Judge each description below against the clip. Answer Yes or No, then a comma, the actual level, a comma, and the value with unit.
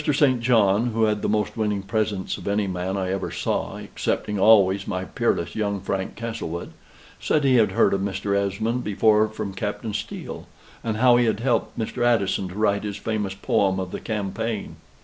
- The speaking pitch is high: No, low, 105 Hz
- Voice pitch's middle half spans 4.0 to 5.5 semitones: No, narrow, 2.4 semitones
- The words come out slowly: No, average, 190 wpm